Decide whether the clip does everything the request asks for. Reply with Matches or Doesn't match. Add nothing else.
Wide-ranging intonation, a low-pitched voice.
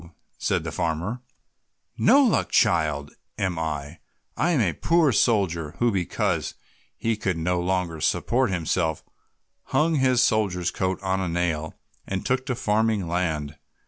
Matches